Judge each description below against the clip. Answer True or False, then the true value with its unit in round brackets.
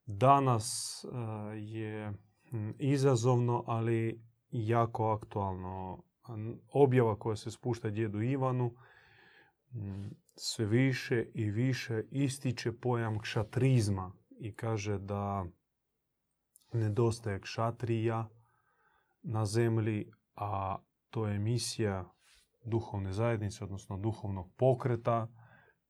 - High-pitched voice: False (115 Hz)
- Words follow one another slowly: True (80 wpm)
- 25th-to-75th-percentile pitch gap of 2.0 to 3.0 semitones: True (2.4 semitones)